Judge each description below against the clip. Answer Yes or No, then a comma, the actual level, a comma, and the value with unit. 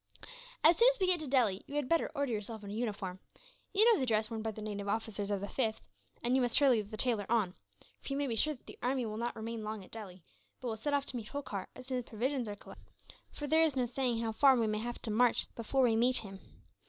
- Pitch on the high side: Yes, high, 235 Hz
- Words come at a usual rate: No, fast, 270 wpm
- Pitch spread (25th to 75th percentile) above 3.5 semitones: Yes, average, 3.9 semitones